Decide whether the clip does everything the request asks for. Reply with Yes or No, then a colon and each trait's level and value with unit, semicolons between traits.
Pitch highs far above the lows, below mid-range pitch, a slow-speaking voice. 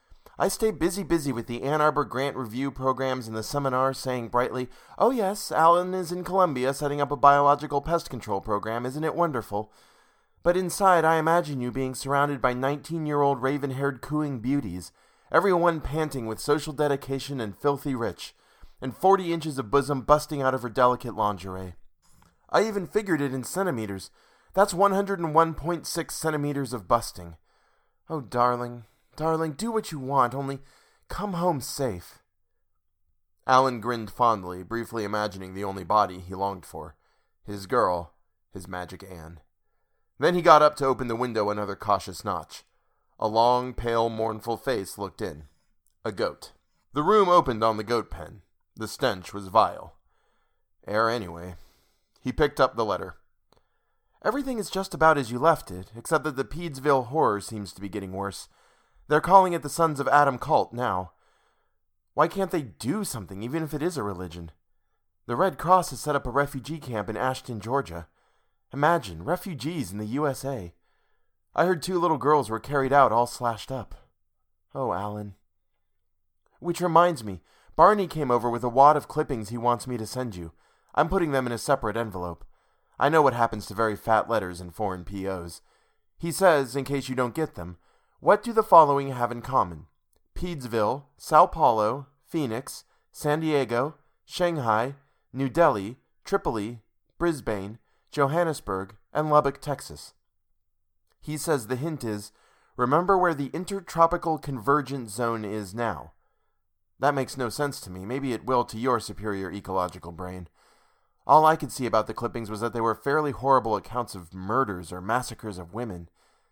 No: wide, 6.5 semitones; low, 125 Hz; average, 165 wpm